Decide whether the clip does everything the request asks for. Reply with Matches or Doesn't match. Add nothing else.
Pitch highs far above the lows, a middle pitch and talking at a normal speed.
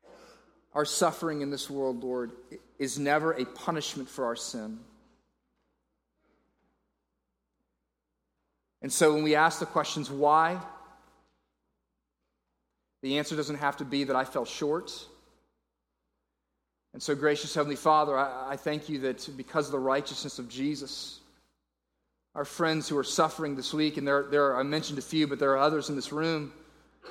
Doesn't match